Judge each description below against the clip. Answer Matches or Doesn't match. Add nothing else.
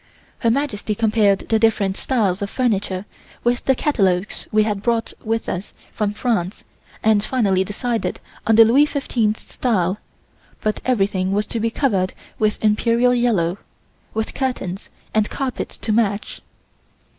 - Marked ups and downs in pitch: Doesn't match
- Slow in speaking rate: Doesn't match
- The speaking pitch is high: Matches